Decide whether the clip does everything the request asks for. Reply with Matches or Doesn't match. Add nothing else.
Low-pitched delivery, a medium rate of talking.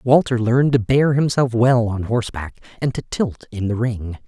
Matches